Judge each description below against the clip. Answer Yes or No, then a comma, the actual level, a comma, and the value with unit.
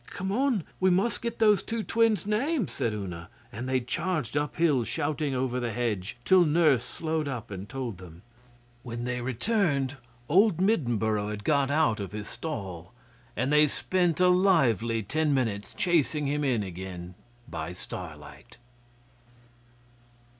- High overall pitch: No, low, 135 Hz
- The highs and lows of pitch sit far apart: Yes, wide, 8.1 semitones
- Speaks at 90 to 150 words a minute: Yes, average, 145 wpm